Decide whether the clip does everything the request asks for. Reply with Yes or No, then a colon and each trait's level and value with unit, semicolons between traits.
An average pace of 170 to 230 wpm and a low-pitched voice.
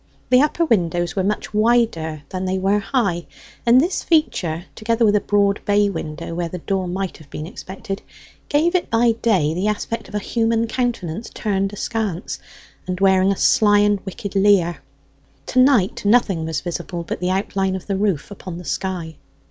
No: average, 180 wpm; high, 195 Hz